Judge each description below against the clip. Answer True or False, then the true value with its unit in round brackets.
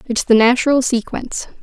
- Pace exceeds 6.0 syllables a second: False (5.8 syllables/s)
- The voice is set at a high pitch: True (245 Hz)